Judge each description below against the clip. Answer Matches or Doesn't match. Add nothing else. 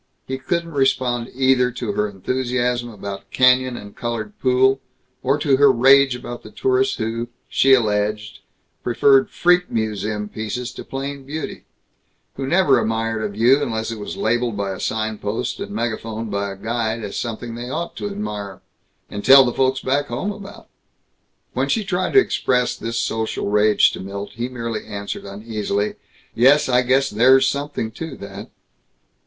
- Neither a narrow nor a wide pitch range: Matches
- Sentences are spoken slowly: Doesn't match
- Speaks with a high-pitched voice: Doesn't match